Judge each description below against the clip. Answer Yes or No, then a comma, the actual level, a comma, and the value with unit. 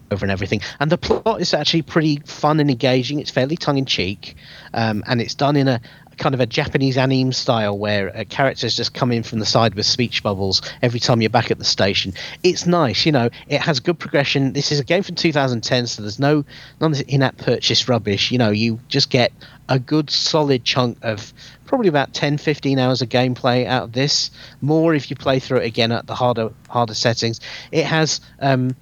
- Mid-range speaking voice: No, low, 130 Hz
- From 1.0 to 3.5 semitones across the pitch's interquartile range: No, average, 3.9 semitones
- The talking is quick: Yes, fast, 215 wpm